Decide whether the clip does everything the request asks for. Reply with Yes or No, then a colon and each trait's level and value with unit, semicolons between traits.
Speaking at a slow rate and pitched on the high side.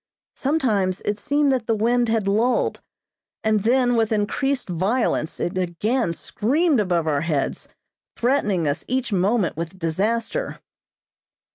Yes: slow, 130 wpm; high, 220 Hz